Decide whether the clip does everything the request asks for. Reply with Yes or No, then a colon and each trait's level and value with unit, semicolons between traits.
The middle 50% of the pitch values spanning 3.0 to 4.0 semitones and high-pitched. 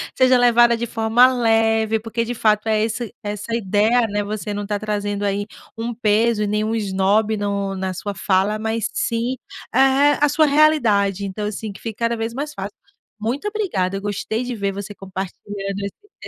No: narrow, 2.6 semitones; high, 215 Hz